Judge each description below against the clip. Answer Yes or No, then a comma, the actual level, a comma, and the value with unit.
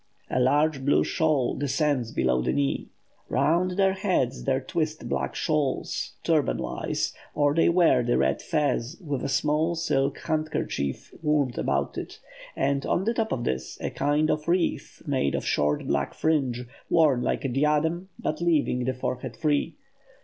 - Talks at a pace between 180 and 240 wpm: No, average, 165 wpm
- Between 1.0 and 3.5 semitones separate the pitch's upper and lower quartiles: No, average, 4.1 semitones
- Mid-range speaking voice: Yes, medium, 145 Hz